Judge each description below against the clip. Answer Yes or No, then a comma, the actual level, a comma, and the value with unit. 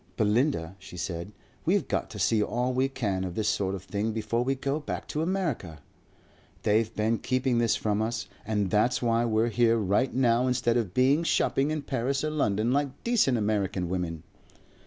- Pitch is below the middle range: Yes, low, 115 Hz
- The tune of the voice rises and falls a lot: No, average, 4.1 semitones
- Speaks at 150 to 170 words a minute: No, average, 185 wpm